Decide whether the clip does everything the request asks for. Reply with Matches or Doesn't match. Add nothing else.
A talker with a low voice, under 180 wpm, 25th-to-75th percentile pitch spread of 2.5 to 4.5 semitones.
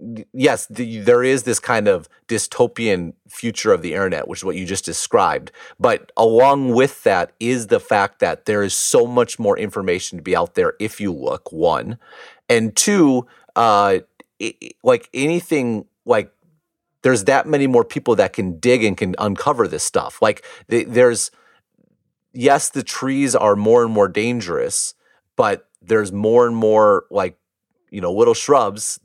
Doesn't match